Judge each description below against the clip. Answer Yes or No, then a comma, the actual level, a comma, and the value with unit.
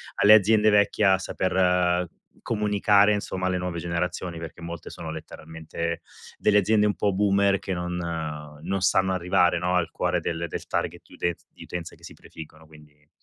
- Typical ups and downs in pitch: Yes, average, 3.0 semitones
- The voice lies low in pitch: Yes, very low, 90 Hz